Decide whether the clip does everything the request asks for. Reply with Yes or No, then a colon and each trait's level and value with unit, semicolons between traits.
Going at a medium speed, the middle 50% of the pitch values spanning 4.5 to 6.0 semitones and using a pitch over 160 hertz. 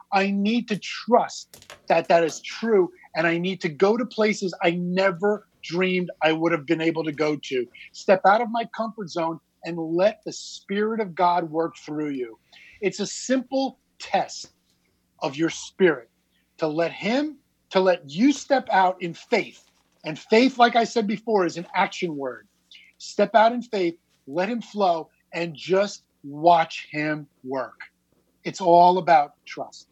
Yes: average, 170 wpm; average, 4.8 semitones; medium, 185 Hz